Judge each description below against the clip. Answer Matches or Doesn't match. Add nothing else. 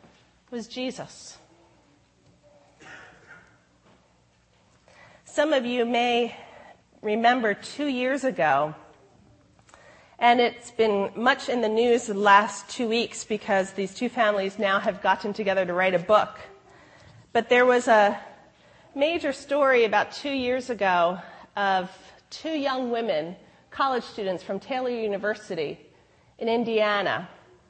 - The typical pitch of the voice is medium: Doesn't match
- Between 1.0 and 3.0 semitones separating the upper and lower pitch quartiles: Doesn't match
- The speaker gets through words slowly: Matches